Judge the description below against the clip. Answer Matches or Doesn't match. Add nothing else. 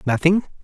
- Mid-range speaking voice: Matches